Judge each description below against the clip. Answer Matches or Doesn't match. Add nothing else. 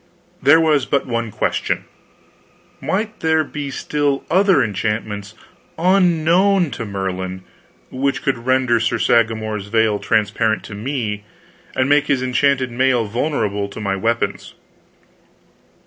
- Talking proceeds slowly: Matches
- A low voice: Matches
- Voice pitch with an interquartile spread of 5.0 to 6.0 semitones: Matches